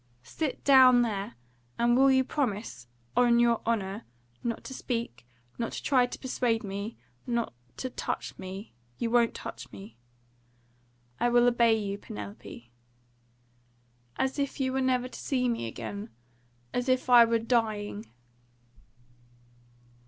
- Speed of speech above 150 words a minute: No, average, 140 wpm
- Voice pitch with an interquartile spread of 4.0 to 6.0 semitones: No, average, 3.6 semitones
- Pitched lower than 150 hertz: No, high, 235 Hz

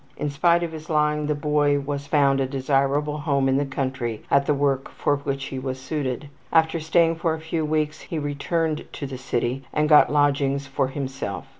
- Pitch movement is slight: Yes, narrow, 2.0 semitones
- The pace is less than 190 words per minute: No, average, 200 wpm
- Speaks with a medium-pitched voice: Yes, medium, 145 Hz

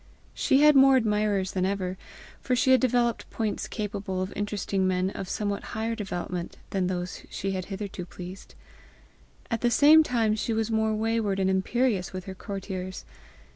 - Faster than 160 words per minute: Yes, average, 170 wpm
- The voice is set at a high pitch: Yes, high, 205 Hz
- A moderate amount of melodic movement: Yes, average, 3.3 semitones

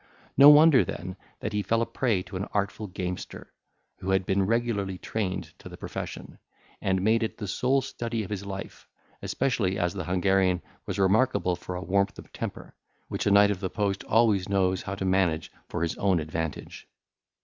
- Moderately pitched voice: No, low, 100 Hz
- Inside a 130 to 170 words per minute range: No, average, 190 wpm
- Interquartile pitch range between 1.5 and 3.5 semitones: Yes, average, 2.8 semitones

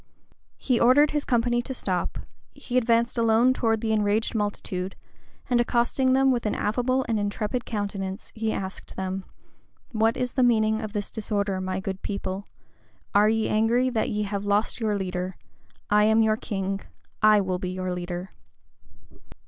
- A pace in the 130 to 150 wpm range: No, average, 165 wpm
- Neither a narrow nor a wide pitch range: Yes, average, 3.2 semitones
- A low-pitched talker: No, high, 215 Hz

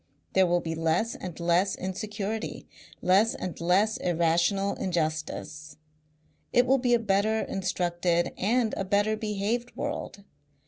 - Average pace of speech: No, slow, 130 wpm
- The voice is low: No, high, 195 Hz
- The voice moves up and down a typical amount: Yes, average, 3.9 semitones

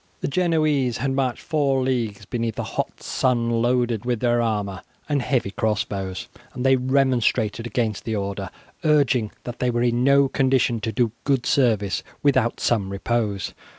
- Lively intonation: No, average, 3.2 semitones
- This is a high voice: No, low, 120 Hz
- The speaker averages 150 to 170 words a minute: Yes, average, 165 wpm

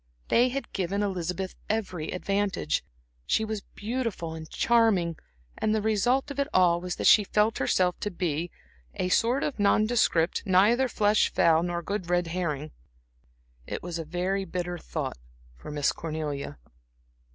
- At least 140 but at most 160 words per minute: Yes, average, 150 wpm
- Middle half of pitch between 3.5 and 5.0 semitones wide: Yes, average, 4.2 semitones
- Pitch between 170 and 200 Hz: Yes, medium, 185 Hz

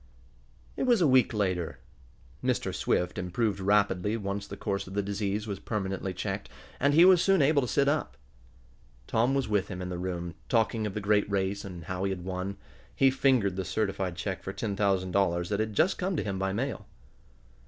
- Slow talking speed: No, fast, 205 wpm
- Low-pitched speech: Yes, low, 100 Hz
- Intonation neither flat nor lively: Yes, average, 3.3 semitones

